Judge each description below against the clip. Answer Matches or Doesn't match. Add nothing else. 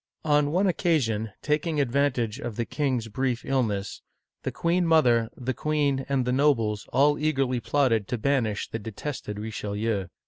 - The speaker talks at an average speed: Matches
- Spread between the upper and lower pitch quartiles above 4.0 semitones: Matches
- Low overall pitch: Matches